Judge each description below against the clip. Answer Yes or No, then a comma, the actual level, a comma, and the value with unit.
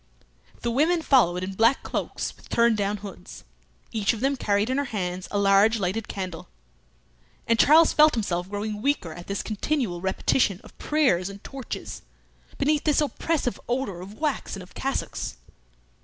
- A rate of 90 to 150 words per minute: No, average, 165 wpm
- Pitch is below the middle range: No, high, 215 Hz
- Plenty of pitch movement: Yes, wide, 5.8 semitones